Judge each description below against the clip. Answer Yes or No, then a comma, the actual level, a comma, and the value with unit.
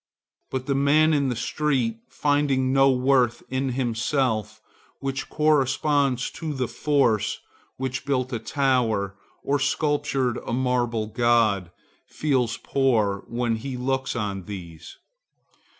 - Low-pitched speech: Yes, low, 130 Hz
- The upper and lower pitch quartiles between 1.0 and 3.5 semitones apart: Yes, average, 3.2 semitones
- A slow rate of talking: Yes, slow, 120 wpm